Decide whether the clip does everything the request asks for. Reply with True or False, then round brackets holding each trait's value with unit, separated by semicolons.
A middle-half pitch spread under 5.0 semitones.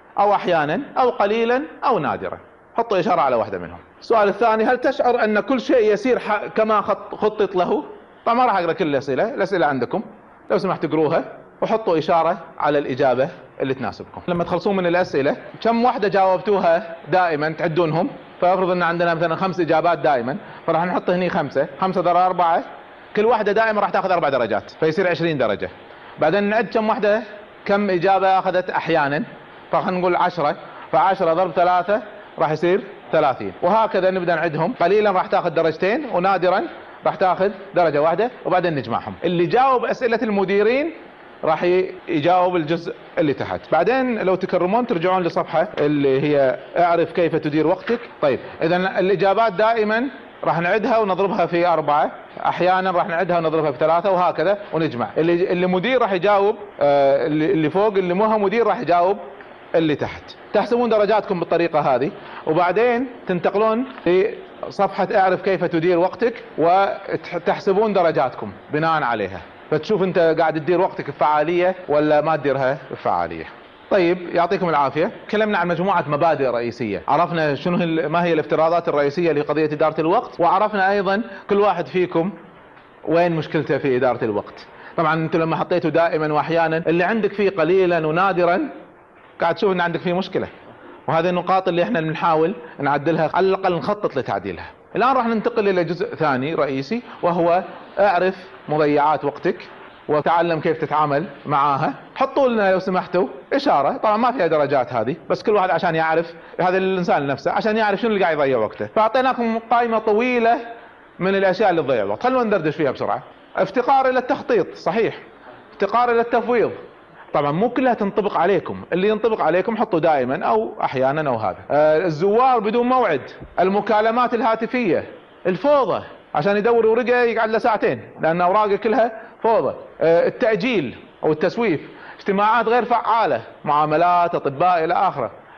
True (4.4 semitones)